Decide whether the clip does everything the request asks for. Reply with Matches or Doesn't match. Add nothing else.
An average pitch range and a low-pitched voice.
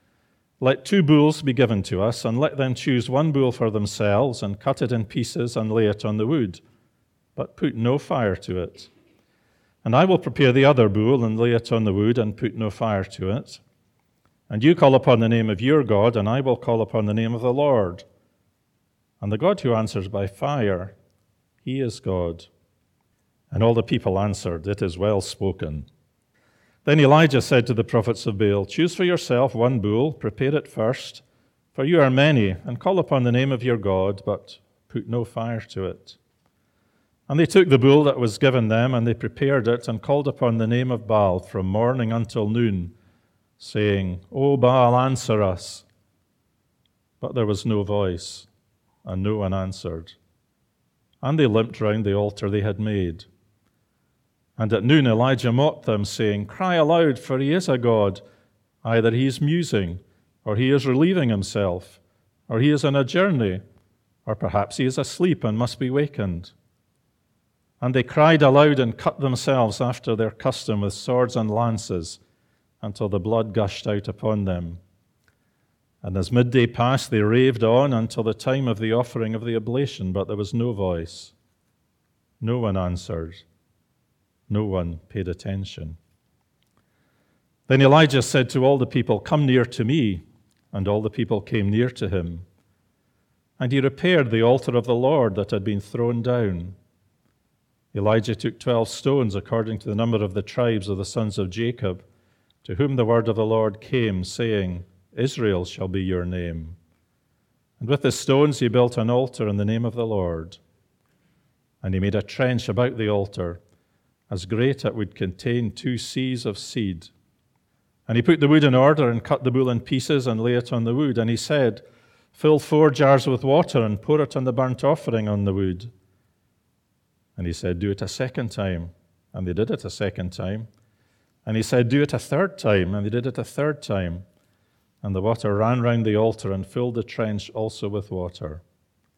Matches